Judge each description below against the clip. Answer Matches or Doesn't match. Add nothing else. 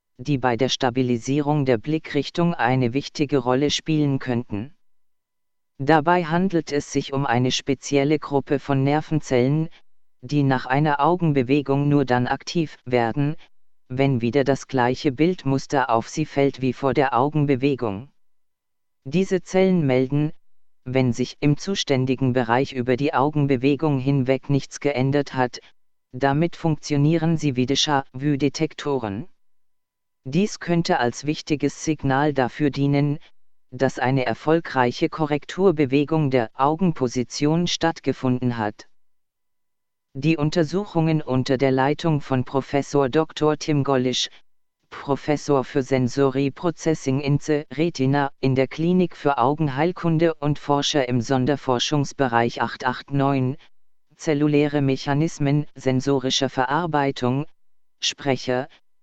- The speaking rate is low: Matches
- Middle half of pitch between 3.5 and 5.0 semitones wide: Doesn't match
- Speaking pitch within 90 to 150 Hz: Matches